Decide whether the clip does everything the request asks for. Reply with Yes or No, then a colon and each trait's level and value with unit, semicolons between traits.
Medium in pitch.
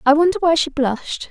No: very high, 310 Hz